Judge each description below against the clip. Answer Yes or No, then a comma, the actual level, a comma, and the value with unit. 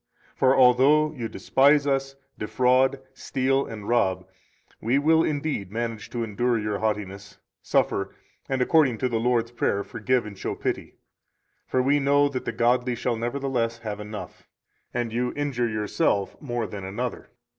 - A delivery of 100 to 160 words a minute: Yes, average, 155 wpm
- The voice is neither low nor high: No, low, 120 Hz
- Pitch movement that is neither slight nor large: Yes, average, 3.7 semitones